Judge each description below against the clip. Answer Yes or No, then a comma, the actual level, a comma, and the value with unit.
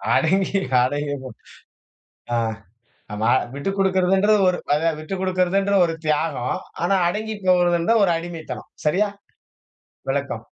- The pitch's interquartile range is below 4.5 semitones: Yes, average, 3.5 semitones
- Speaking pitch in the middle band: Yes, medium, 180 Hz